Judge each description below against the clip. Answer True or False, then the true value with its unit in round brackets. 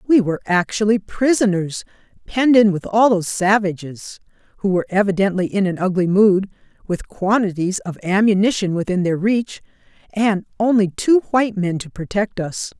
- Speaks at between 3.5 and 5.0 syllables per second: False (5.2 syllables/s)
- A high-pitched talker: True (200 Hz)